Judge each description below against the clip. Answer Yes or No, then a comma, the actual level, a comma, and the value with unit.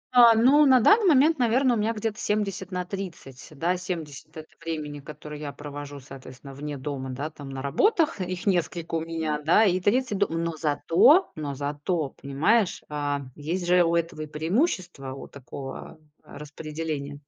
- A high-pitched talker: No, medium, 165 Hz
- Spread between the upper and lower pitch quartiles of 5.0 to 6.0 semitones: Yes, wide, 5.5 semitones